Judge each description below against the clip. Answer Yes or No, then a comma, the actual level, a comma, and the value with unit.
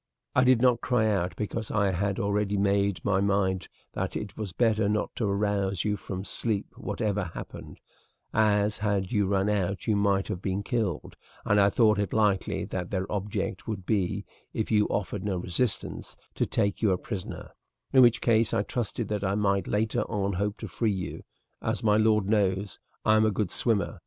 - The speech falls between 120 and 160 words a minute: No, average, 195 wpm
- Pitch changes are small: Yes, narrow, 1.8 semitones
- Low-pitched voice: Yes, low, 100 Hz